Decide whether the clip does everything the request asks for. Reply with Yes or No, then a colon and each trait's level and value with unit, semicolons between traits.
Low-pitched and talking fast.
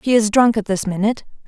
No: high, 215 Hz; fast, 245 wpm